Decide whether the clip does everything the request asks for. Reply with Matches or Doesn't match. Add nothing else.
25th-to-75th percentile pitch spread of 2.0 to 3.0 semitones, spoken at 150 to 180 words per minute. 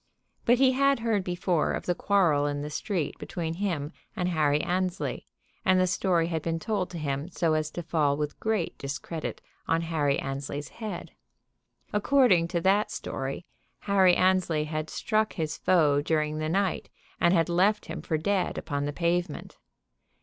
Doesn't match